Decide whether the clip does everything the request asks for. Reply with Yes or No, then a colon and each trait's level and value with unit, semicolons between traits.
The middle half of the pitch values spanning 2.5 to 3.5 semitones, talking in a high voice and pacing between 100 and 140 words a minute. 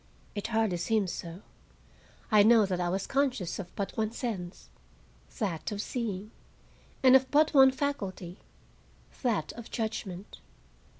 No: average, 4.6 semitones; high, 215 Hz; slow, 135 wpm